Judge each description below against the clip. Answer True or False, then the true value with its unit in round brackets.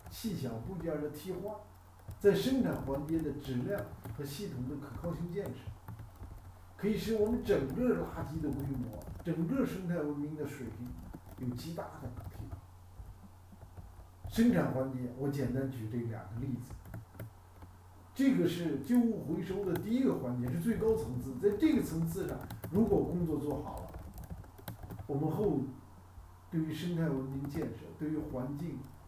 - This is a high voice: False (130 Hz)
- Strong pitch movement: True (8.5 semitones)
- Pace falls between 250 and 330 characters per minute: False (225 characters per minute)